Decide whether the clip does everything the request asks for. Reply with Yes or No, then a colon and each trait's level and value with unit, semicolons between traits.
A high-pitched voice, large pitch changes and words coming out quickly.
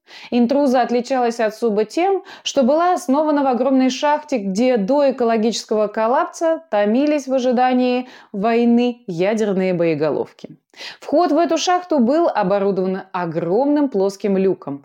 No: very high, 250 Hz; wide, 5.7 semitones; average, 120 wpm